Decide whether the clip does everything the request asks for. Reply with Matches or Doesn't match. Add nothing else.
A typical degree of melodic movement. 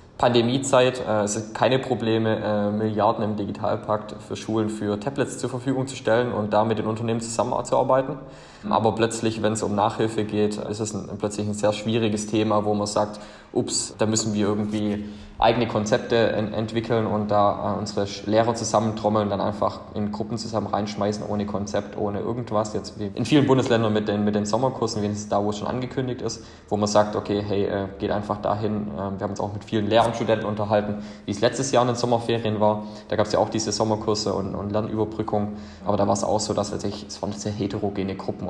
Doesn't match